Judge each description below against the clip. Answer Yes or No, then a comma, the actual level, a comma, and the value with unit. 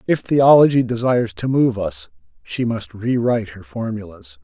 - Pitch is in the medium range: No, low, 110 Hz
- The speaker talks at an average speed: Yes, average, 160 wpm